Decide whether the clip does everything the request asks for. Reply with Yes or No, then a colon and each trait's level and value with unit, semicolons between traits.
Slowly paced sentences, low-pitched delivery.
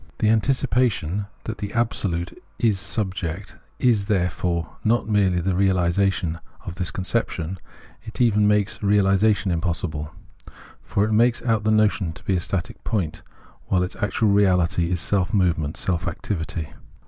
No: average, 150 wpm; very low, 95 Hz